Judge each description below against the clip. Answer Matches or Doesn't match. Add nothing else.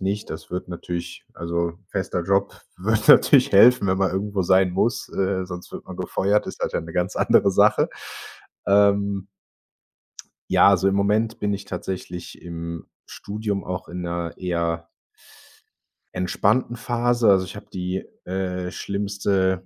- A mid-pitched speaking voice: Doesn't match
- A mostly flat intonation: Matches